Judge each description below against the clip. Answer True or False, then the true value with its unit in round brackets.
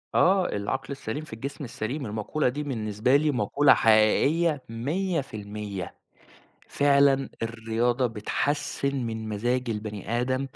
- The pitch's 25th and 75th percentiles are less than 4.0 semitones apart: False (4.6 semitones)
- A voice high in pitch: False (125 Hz)